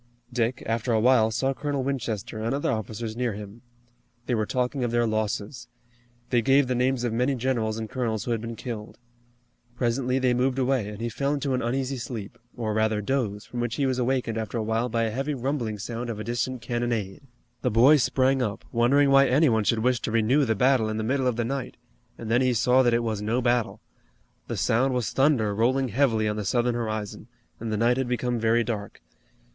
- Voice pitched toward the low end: Yes, low, 120 Hz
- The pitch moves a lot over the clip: No, average, 2.7 semitones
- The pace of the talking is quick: Yes, fast, 220 wpm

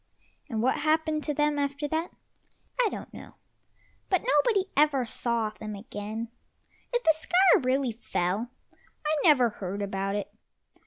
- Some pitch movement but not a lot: No, wide, 6.5 semitones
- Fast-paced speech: No, average, 145 wpm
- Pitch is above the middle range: Yes, very high, 265 Hz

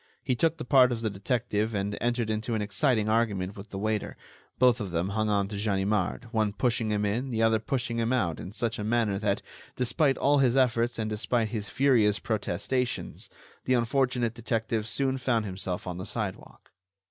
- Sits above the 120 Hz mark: No, low, 110 Hz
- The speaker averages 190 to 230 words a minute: Yes, average, 195 wpm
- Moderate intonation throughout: Yes, average, 3.0 semitones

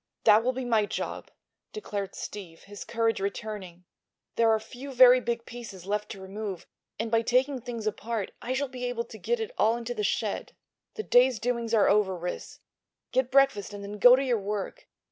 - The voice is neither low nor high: No, high, 225 Hz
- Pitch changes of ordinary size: Yes, average, 3.3 semitones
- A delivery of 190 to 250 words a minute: Yes, average, 195 wpm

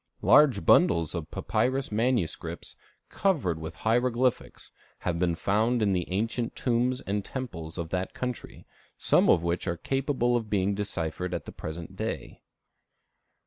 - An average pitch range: No, wide, 6.4 semitones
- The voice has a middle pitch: No, low, 105 Hz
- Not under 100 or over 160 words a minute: Yes, average, 145 wpm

